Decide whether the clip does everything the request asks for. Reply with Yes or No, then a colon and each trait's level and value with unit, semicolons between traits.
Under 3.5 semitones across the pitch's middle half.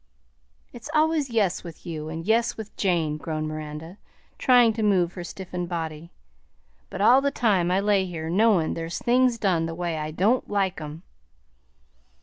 No: average, 5.2 semitones